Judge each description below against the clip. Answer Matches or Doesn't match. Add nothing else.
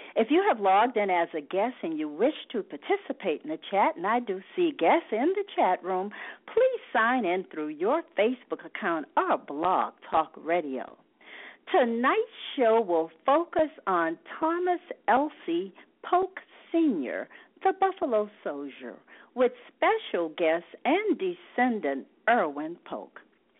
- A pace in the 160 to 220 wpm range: Doesn't match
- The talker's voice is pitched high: Matches